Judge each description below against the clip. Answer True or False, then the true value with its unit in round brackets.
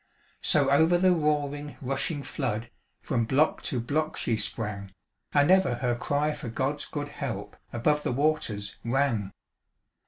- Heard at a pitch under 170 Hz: True (140 Hz)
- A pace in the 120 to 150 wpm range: True (145 wpm)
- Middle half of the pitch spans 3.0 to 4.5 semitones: True (4.1 semitones)